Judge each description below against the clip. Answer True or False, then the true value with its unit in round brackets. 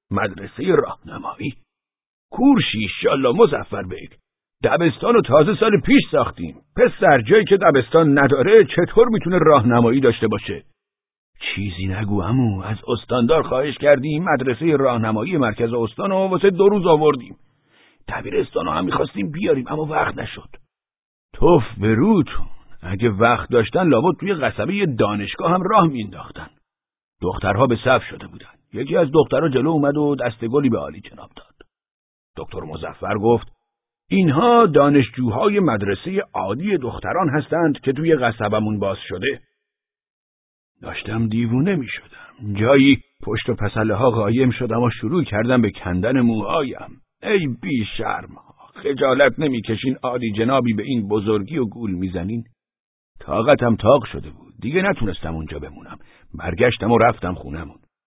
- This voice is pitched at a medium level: False (120 Hz)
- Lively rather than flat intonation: True (6.2 semitones)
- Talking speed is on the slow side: False (135 wpm)